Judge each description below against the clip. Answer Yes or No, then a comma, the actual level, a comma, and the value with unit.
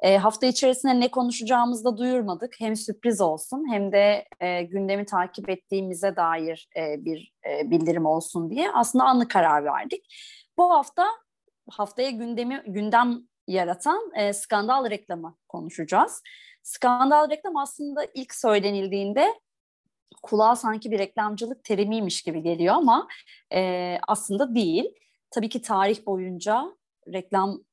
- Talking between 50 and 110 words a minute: No, average, 125 wpm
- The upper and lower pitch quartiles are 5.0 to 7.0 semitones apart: Yes, wide, 5.4 semitones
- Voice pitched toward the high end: Yes, high, 220 Hz